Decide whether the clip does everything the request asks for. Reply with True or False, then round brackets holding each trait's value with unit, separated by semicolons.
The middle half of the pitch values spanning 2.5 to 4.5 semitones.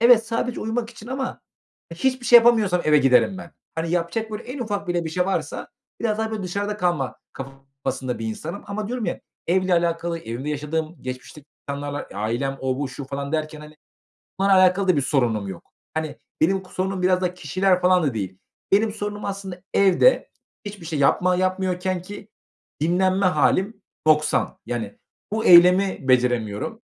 False (5.6 semitones)